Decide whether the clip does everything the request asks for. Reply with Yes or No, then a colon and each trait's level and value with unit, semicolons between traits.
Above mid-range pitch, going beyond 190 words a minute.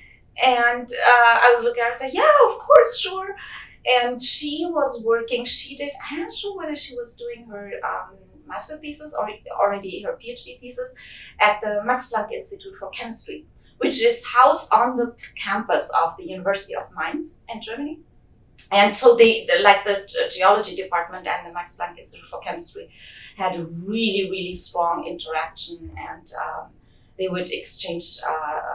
No: high, 240 Hz; average, 175 wpm